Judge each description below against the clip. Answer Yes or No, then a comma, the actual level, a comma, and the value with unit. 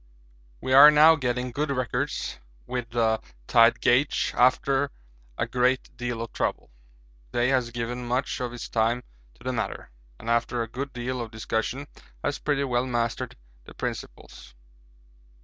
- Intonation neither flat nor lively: No, narrow, 1.9 semitones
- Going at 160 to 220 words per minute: No, average, 150 wpm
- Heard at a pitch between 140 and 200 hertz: No, low, 125 Hz